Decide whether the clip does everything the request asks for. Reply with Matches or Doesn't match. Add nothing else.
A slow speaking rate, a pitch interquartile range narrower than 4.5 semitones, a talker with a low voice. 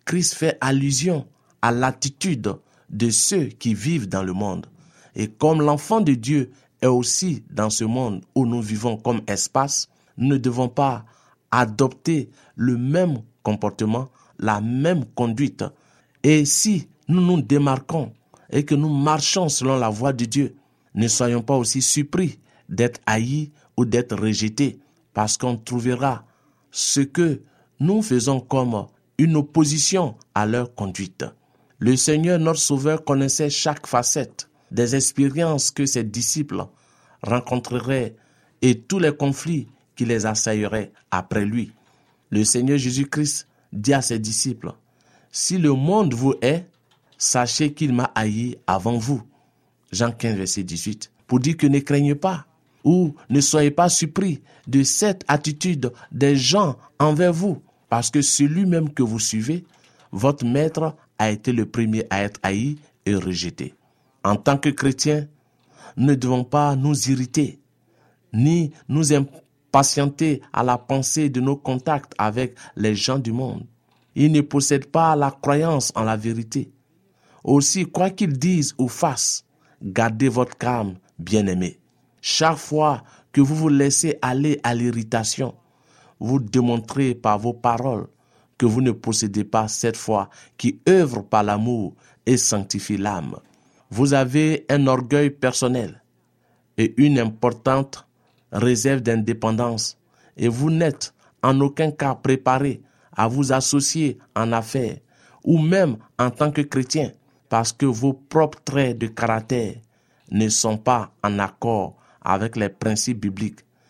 Matches